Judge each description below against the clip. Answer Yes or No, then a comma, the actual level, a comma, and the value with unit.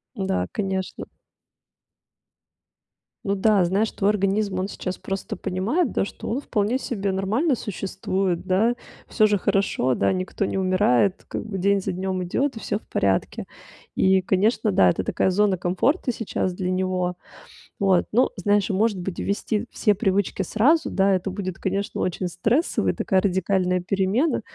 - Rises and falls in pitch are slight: Yes, narrow, 2.2 semitones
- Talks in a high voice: Yes, high, 195 Hz